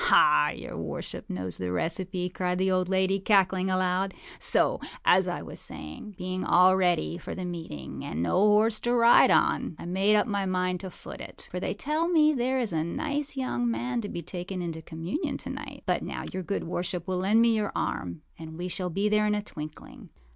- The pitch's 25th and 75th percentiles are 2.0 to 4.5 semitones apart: Yes, average, 3.4 semitones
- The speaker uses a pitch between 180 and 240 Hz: Yes, medium, 185 Hz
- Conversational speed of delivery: No, fast, 210 wpm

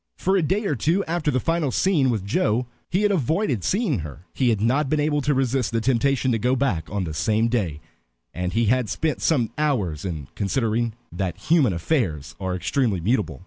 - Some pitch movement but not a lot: No, wide, 7.0 semitones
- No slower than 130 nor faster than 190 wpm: No, fast, 205 wpm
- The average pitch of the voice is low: Yes, low, 120 Hz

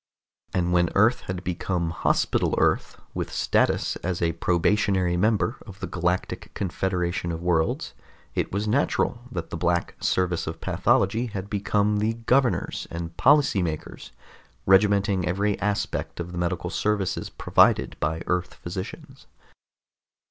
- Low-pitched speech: Yes, very low, 95 Hz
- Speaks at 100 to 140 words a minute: Yes, slow, 135 wpm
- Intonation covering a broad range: No, average, 3.0 semitones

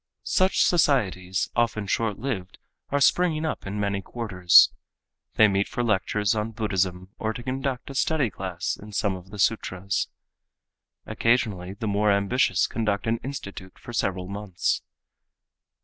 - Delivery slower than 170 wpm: Yes, average, 145 wpm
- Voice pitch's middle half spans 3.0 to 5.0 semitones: Yes, average, 3.8 semitones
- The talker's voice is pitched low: Yes, low, 105 Hz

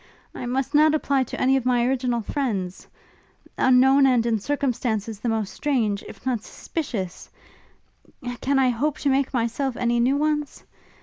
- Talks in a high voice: Yes, very high, 255 Hz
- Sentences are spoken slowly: No, average, 160 wpm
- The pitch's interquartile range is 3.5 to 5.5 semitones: No, average, 3.1 semitones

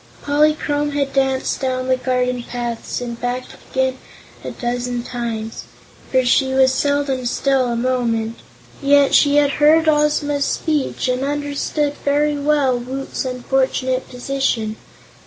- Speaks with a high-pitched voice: Yes, very high, 265 Hz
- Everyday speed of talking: No, slow, 130 wpm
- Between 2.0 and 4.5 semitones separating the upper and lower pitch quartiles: Yes, narrow, 2.6 semitones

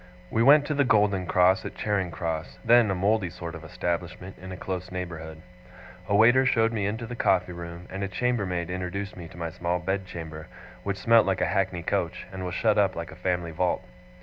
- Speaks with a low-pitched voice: Yes, very low, 95 Hz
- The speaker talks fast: Yes, fast, 210 wpm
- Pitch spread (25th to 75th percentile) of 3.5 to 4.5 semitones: No, average, 2.9 semitones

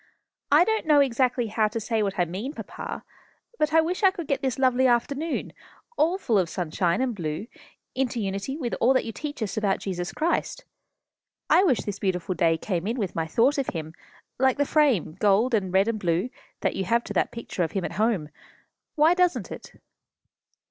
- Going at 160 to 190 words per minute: No, fast, 205 wpm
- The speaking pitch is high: Yes, high, 230 Hz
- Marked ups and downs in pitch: Yes, wide, 6.7 semitones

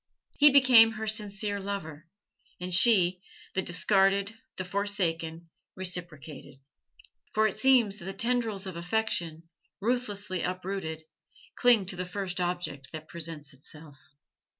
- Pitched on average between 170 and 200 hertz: Yes, high, 190 Hz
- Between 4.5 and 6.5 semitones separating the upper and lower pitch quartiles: No, average, 3.7 semitones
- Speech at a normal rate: No, slow, 125 wpm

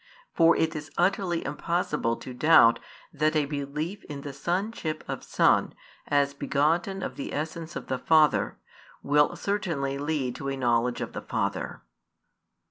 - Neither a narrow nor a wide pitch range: Yes, average, 3.2 semitones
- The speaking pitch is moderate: Yes, medium, 150 Hz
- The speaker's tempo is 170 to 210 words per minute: No, average, 150 wpm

